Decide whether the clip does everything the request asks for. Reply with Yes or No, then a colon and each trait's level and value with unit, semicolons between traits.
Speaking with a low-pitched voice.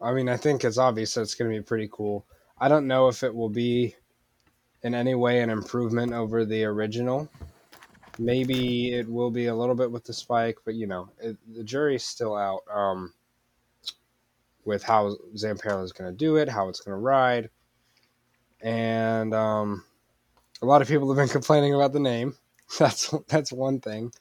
Yes: low, 120 Hz